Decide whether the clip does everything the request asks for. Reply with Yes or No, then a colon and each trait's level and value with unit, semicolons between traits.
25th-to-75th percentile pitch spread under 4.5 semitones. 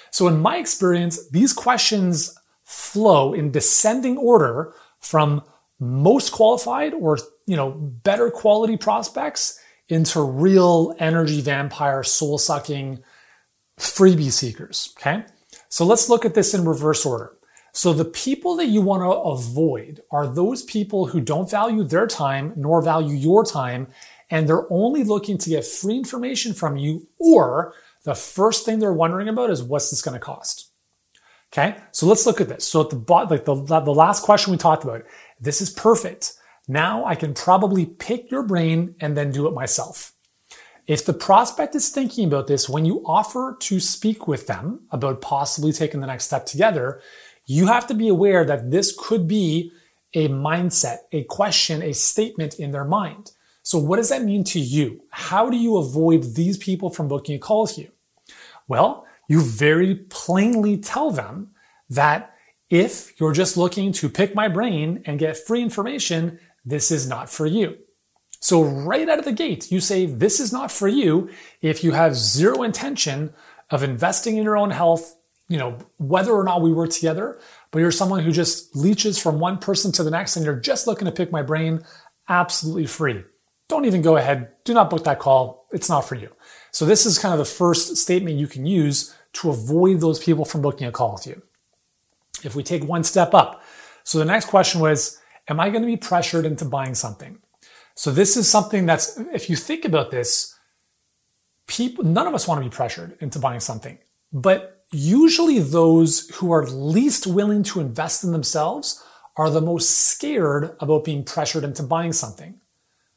No: average, 5.1 semitones